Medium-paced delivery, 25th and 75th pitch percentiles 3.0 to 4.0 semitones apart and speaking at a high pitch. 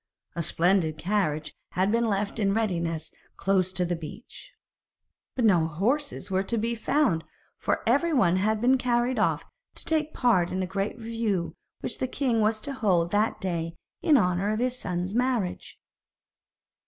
No: average, 165 wpm; average, 5.0 semitones; high, 205 Hz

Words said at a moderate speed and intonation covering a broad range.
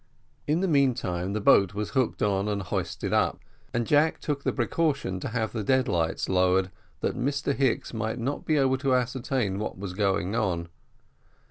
Yes: average, 180 wpm; wide, 5.8 semitones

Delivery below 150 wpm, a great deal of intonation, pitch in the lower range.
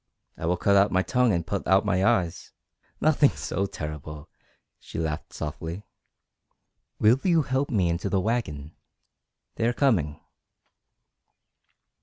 Yes: average, 140 wpm; wide, 6.0 semitones; very low, 95 Hz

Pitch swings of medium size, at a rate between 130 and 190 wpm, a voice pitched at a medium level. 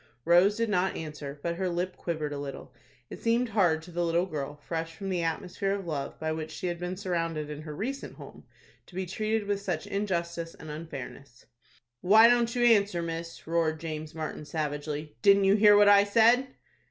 No: average, 4.2 semitones; average, 200 wpm; medium, 170 Hz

